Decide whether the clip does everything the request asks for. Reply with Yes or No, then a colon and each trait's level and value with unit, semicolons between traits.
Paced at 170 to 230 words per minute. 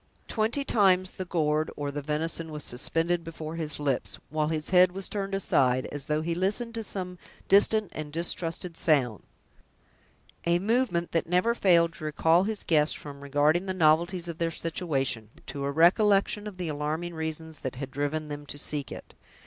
Yes: average, 175 wpm